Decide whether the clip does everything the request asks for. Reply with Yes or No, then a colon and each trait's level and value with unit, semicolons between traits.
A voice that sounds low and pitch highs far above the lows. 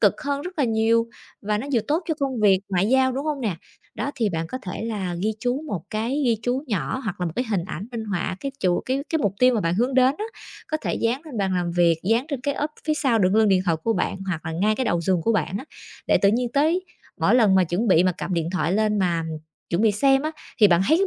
No: high, 220 Hz; wide, 6.1 semitones